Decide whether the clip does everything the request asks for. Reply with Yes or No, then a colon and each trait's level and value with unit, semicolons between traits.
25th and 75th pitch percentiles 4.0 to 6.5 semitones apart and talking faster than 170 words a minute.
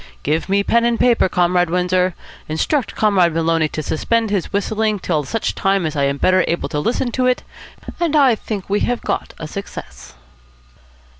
Yes: wide, 5.5 semitones; average, 180 wpm